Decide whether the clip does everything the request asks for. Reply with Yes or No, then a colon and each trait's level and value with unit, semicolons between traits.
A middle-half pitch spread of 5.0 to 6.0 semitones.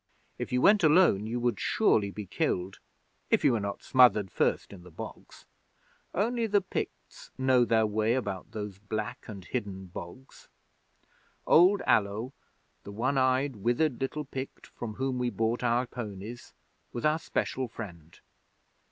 No: average, 4.3 semitones